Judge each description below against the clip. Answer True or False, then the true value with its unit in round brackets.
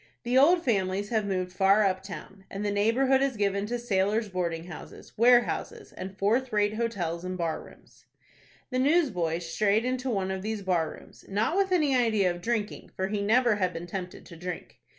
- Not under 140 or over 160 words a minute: False (190 wpm)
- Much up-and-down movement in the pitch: False (4.2 semitones)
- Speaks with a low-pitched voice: False (205 Hz)